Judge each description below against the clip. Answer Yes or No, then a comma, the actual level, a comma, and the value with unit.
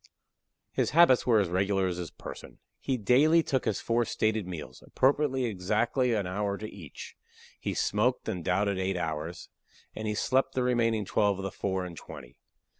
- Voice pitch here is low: Yes, low, 105 Hz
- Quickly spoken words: No, average, 180 wpm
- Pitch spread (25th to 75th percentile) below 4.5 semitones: No, average, 5.0 semitones